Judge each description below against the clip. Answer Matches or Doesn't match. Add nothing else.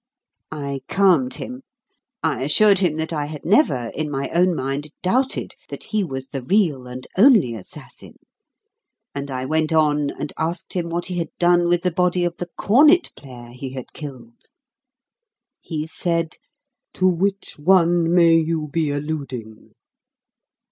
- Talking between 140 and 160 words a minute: Matches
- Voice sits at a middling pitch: Matches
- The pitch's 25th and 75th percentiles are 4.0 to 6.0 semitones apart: Matches